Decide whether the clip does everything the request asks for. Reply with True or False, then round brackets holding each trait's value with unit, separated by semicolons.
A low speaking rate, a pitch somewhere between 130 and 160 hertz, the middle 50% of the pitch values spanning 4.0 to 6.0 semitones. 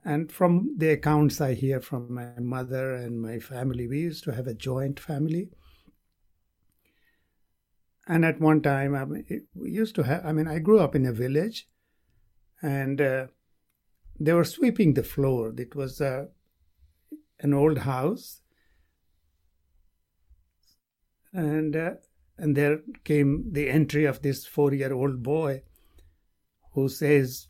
False (145 wpm; 135 Hz; 5.1 semitones)